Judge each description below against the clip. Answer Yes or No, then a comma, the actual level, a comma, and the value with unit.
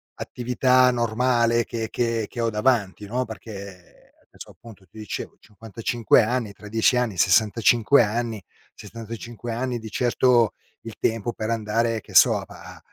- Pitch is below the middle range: Yes, low, 115 Hz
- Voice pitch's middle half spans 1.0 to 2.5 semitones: Yes, narrow, 2.0 semitones